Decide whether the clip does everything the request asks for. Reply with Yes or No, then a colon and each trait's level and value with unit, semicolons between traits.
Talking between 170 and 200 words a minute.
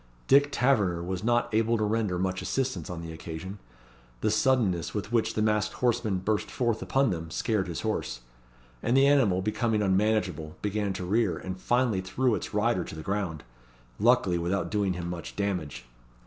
Yes: average, 175 wpm